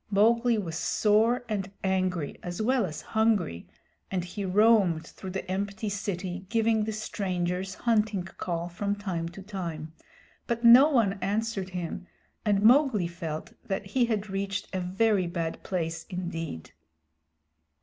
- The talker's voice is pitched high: Yes, high, 195 Hz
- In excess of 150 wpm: No, average, 140 wpm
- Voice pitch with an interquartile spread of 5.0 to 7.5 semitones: No, average, 3.4 semitones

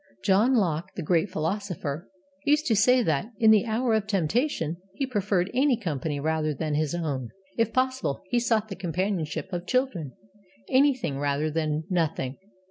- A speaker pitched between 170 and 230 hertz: Yes, medium, 185 Hz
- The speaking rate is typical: Yes, average, 160 wpm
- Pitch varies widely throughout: Yes, wide, 6.6 semitones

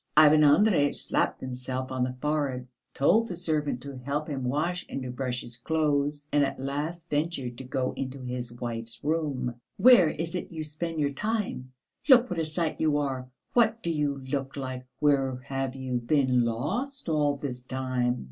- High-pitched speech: No, medium, 140 Hz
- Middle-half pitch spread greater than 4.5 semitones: No, average, 3.6 semitones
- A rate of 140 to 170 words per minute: No, average, 180 wpm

